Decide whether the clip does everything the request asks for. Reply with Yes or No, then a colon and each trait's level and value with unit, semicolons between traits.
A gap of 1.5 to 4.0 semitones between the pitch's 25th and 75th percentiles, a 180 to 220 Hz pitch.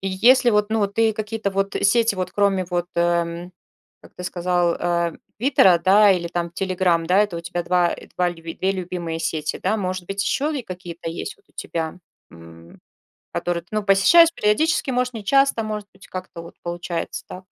Yes: average, 3.4 semitones; medium, 185 Hz